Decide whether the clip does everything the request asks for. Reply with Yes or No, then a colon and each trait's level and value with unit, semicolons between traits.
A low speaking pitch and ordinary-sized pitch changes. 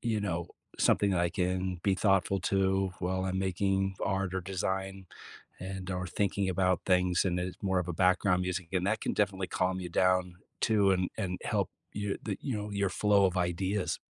No: very low, 95 Hz; narrow, 1.3 semitones